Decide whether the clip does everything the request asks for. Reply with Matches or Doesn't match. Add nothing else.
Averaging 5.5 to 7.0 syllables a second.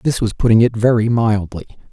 Matches